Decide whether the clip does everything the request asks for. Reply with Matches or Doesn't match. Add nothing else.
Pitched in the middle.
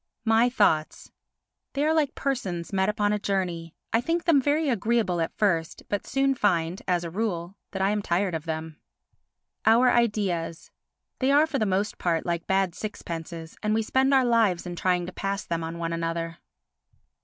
Doesn't match